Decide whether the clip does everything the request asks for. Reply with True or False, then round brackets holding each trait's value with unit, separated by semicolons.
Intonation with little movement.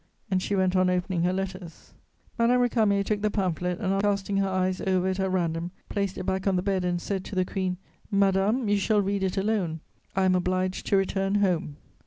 True (1.5 semitones)